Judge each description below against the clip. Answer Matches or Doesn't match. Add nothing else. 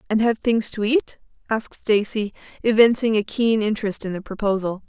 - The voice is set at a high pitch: Matches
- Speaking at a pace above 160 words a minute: Matches